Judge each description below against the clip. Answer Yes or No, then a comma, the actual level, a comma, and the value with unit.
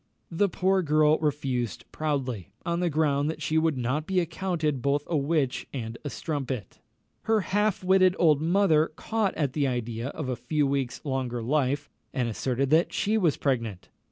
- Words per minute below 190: Yes, average, 175 wpm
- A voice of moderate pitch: Yes, medium, 150 Hz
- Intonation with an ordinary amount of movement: Yes, average, 4.3 semitones